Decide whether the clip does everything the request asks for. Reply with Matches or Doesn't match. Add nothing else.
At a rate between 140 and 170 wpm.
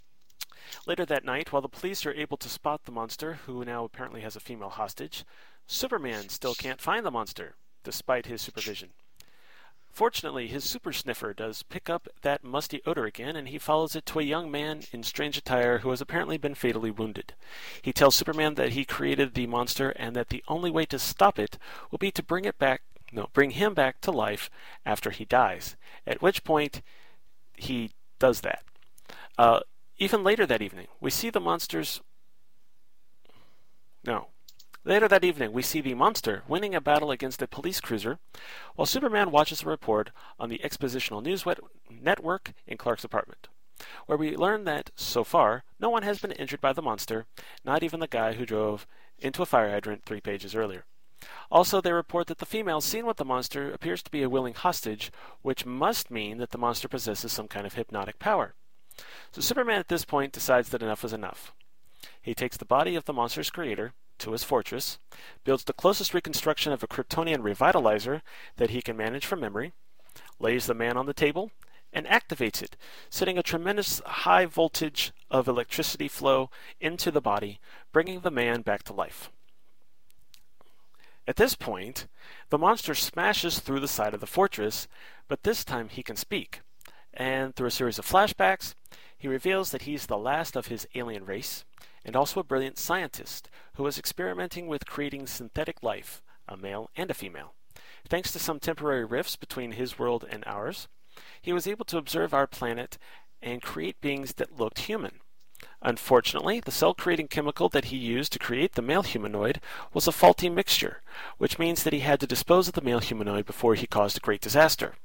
Doesn't match